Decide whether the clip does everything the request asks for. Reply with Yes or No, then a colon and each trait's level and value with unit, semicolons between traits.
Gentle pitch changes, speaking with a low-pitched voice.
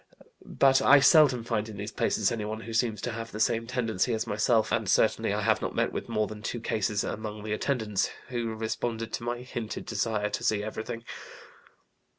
Yes: narrow, 1.7 semitones; low, 110 Hz